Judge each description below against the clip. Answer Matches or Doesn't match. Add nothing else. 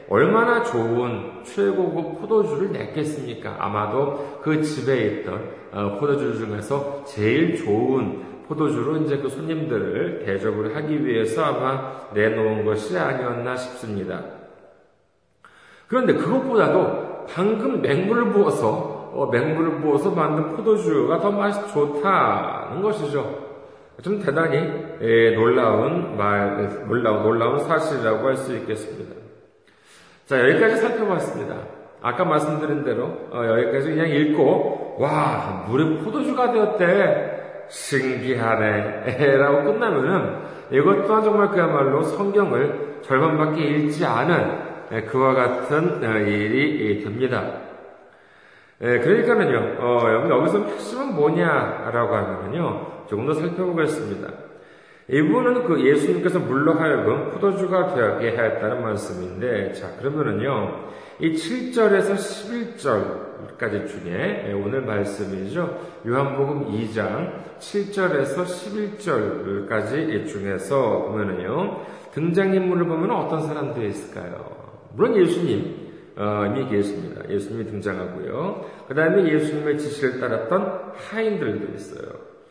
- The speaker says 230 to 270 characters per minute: Matches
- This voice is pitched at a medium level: Matches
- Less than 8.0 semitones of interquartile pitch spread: Doesn't match